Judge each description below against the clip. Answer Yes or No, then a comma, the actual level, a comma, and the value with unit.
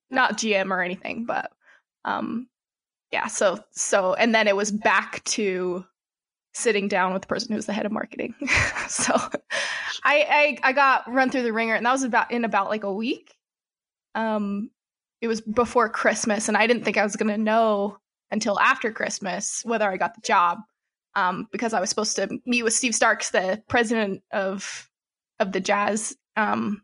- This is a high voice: Yes, high, 220 Hz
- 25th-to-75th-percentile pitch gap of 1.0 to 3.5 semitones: Yes, average, 2.8 semitones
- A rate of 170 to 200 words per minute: Yes, average, 185 wpm